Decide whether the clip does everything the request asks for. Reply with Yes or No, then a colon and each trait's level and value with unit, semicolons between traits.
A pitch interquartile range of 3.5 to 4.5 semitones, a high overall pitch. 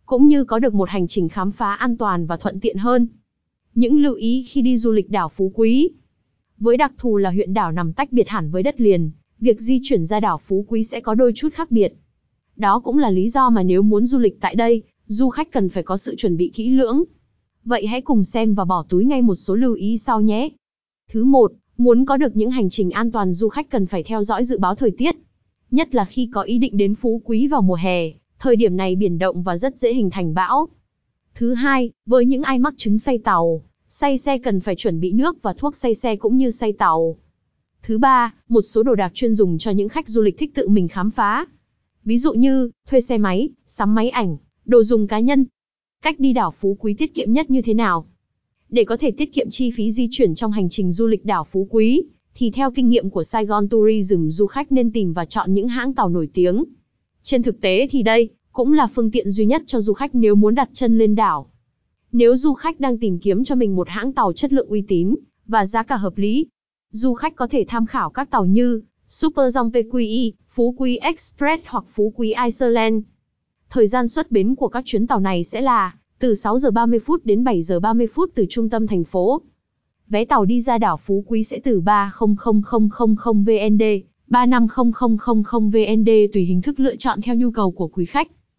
Yes: average, 3.8 semitones; high, 225 Hz